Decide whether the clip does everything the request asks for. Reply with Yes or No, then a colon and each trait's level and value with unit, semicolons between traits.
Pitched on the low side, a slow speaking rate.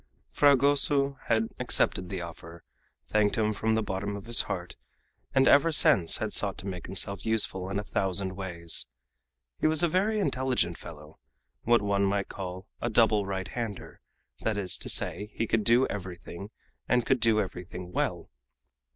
No: low, 100 Hz; average, 170 wpm